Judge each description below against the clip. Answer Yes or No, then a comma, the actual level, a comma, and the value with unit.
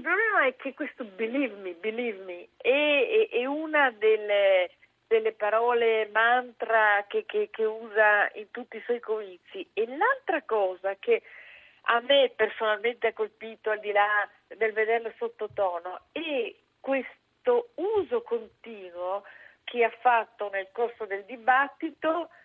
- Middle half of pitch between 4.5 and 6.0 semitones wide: Yes, wide, 5.4 semitones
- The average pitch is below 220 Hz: No, high, 230 Hz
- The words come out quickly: No, average, 135 wpm